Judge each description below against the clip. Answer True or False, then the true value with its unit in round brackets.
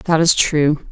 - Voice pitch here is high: False (155 Hz)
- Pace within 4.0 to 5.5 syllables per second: False (3.5 syllables/s)